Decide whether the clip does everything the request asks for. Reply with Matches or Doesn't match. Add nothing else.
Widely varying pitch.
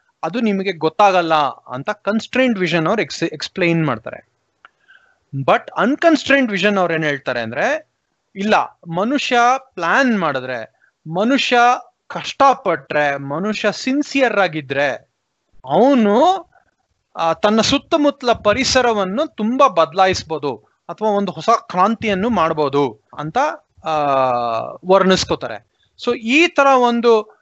Matches